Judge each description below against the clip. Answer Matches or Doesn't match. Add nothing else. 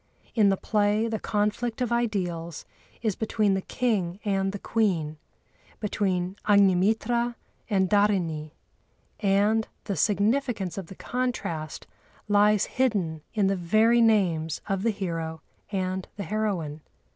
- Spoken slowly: Matches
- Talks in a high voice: Matches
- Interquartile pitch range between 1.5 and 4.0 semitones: Matches